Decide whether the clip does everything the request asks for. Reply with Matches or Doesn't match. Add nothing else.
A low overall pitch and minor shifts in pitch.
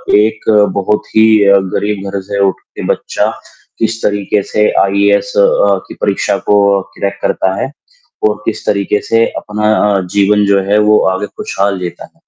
Matches